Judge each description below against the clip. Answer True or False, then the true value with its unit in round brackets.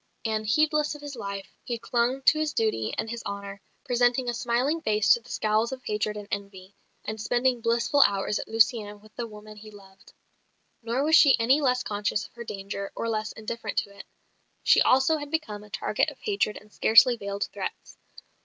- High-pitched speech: True (225 Hz)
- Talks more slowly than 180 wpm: False (200 wpm)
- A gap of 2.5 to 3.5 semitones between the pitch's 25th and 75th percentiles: True (3.2 semitones)